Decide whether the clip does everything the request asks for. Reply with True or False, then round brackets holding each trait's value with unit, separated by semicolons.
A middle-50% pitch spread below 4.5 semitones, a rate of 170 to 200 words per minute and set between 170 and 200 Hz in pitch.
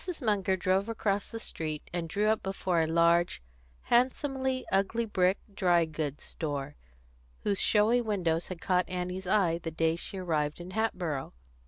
False (4.0 semitones; 155 wpm; 185 Hz)